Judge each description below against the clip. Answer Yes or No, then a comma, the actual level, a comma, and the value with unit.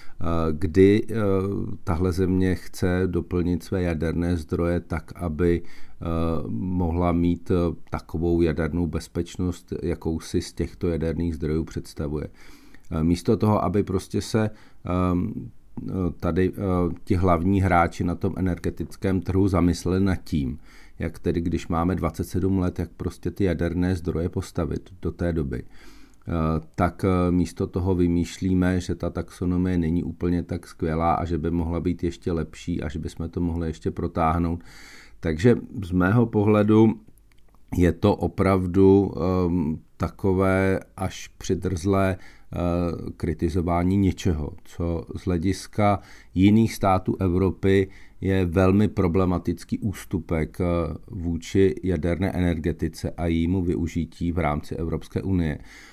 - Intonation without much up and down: Yes, narrow, 2.0 semitones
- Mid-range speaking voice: No, very low, 90 Hz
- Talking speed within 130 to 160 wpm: No, average, 120 wpm